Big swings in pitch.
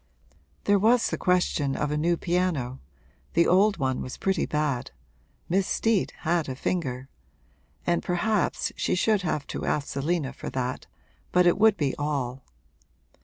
No: average, 5.0 semitones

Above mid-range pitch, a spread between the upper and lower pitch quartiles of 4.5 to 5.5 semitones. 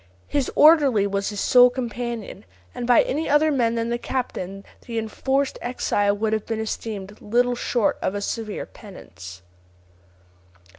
No: high, 230 Hz; average, 3.4 semitones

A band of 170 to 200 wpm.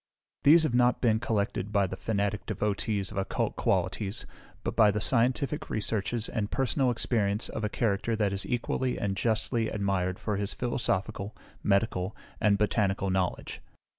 No: average, 155 wpm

